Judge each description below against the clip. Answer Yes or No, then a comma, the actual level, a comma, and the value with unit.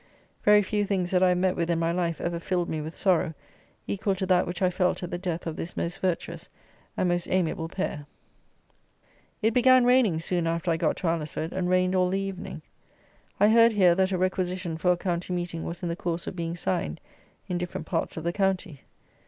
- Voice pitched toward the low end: No, medium, 180 Hz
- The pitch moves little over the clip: Yes, narrow, 1.9 semitones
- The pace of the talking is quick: Yes, fast, 220 wpm